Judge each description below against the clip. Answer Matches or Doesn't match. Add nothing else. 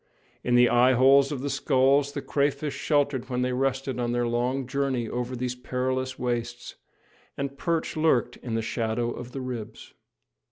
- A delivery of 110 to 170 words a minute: Matches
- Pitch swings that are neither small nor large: Doesn't match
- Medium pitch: Doesn't match